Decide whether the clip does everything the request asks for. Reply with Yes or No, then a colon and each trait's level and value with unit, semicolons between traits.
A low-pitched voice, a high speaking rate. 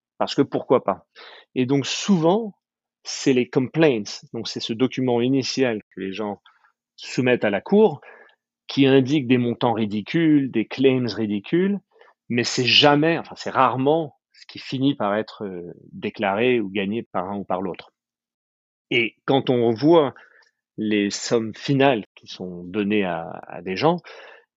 No: low, 125 Hz; average, 155 wpm